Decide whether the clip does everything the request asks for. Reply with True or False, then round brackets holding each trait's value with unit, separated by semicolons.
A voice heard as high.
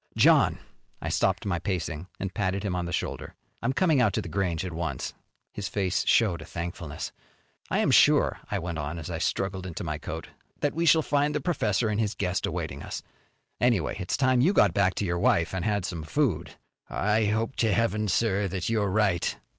False (95 Hz)